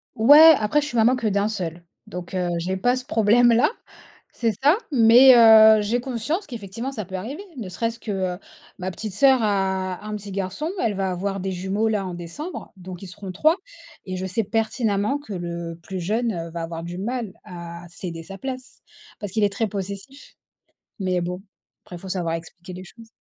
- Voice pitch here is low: No, high, 200 Hz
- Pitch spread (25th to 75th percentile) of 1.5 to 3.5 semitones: No, average, 4.1 semitones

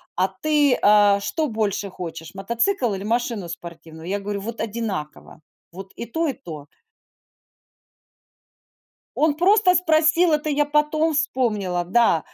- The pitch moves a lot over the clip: Yes, wide, 8.0 semitones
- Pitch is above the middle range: Yes, high, 225 Hz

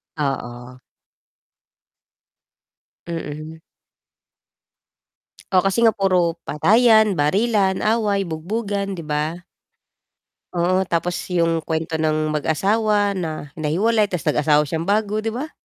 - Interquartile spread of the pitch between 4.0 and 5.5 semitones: Yes, average, 4.7 semitones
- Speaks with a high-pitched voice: No, medium, 180 Hz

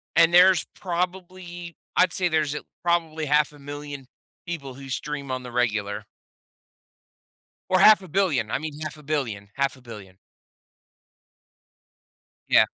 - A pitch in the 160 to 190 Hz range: No, medium, 150 Hz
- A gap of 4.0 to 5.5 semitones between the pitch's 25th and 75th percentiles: Yes, average, 4.4 semitones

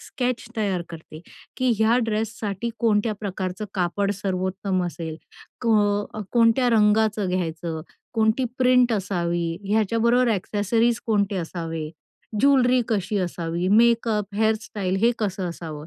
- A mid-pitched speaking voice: No, high, 205 Hz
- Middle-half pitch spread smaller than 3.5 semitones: No, average, 3.8 semitones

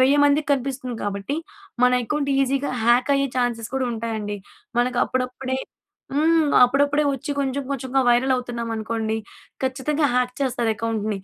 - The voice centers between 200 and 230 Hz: No, very high, 255 Hz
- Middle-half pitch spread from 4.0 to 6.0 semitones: No, average, 2.9 semitones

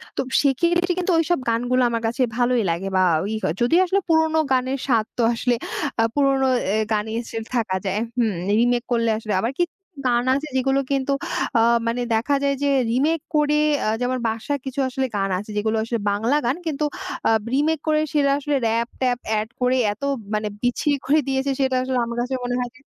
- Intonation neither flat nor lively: Yes, average, 3.5 semitones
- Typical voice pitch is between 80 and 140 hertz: No, very high, 255 Hz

